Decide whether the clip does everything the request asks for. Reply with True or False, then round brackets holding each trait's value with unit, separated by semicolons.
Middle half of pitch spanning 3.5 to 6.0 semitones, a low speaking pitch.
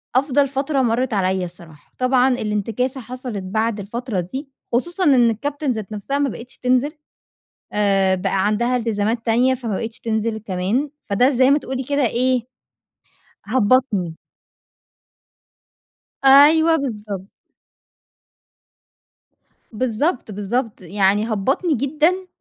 False (4.4 semitones; 235 Hz)